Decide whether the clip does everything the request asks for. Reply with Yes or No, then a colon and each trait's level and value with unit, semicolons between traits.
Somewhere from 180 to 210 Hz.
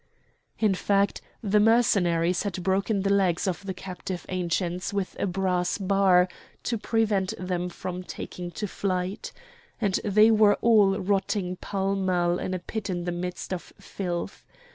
Yes: high, 190 Hz